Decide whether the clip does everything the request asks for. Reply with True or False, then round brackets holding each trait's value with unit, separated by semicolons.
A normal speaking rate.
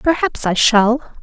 True (145 wpm)